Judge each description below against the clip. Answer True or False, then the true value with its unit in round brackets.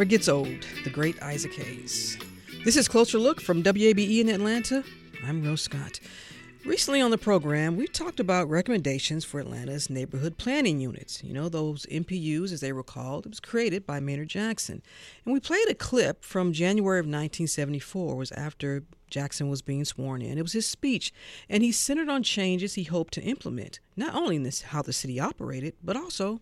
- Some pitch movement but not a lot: False (7.5 semitones)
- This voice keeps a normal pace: True (190 wpm)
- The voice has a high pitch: False (165 Hz)